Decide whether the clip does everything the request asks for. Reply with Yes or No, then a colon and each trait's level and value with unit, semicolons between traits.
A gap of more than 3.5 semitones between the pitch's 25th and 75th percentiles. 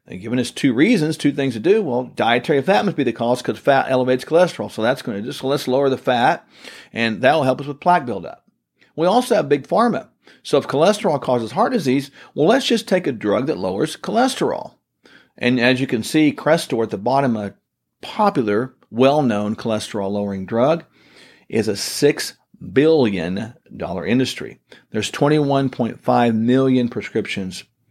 Yes: average, 4.0 semitones